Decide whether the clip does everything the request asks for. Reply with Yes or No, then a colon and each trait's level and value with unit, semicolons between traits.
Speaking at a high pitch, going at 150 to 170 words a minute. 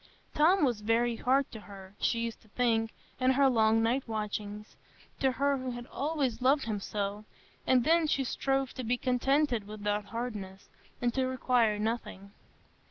Yes: high, 240 Hz; average, 165 wpm